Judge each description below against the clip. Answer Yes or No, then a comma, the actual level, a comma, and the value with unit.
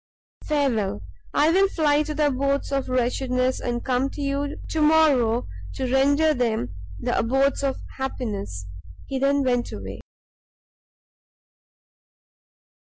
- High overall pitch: Yes, very high, 270 Hz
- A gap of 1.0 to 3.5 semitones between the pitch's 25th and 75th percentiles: Yes, average, 2.9 semitones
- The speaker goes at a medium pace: No, slow, 120 wpm